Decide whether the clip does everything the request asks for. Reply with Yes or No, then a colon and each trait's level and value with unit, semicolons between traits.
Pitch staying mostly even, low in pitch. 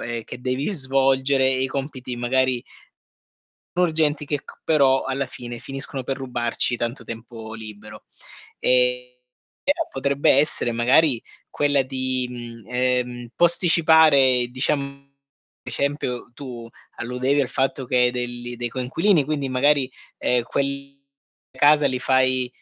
Yes: narrow, 2.2 semitones; low, 130 Hz